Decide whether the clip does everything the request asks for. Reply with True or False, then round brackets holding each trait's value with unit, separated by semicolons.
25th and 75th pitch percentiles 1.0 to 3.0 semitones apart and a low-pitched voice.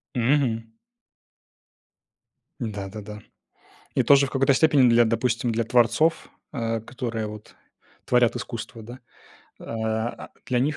True (2.5 semitones; 120 Hz)